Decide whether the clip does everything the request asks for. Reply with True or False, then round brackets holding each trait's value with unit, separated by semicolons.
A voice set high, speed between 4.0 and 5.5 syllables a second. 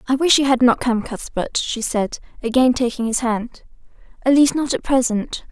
True (245 Hz; 4.9 syllables/s)